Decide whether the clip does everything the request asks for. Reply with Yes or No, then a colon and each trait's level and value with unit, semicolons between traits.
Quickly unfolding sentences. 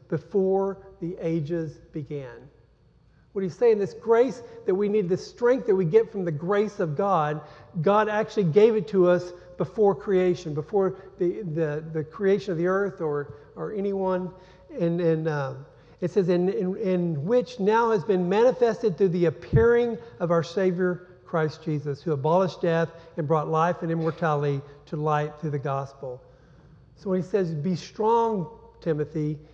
No: average, 165 wpm